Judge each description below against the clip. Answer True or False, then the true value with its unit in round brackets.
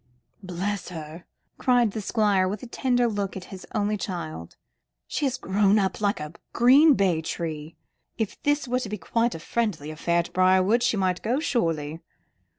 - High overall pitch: True (200 Hz)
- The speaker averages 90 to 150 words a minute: False (180 wpm)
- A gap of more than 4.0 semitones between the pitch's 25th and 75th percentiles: True (5.3 semitones)